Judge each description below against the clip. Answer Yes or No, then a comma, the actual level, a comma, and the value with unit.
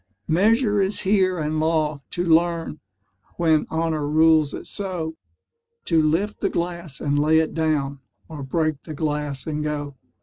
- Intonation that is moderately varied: No, narrow, 2.3 semitones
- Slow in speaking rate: No, average, 155 wpm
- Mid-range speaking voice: Yes, medium, 160 Hz